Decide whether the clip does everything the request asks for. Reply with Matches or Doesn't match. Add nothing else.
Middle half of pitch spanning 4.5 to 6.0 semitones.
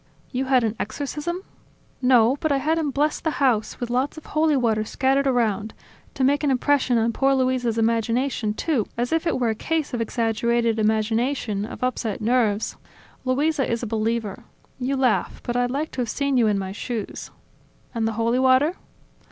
Doesn't match